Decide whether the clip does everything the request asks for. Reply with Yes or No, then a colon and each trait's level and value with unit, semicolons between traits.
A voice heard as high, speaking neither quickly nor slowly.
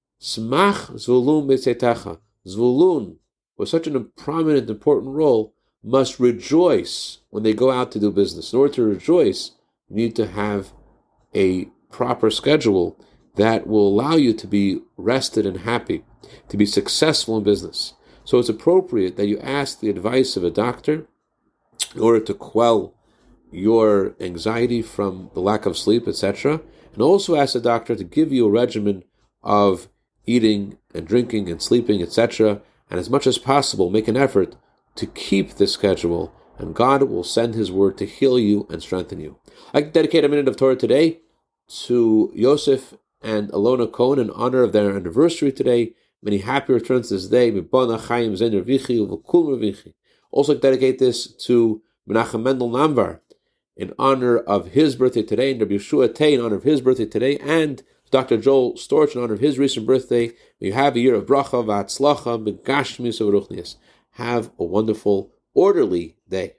No: low, 120 Hz; average, 155 wpm